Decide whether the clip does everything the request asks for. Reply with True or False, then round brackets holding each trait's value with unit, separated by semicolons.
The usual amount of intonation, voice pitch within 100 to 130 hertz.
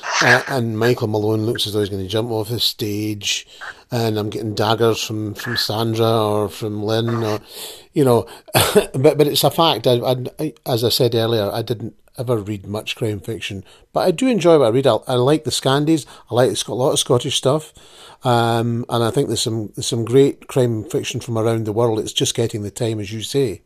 True (3.3 semitones; 115 Hz)